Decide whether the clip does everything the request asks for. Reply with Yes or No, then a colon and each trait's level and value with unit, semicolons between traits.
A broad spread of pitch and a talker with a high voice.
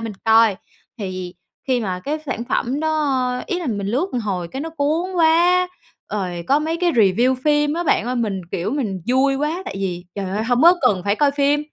Yes: wide, 6.9 semitones; very high, 255 Hz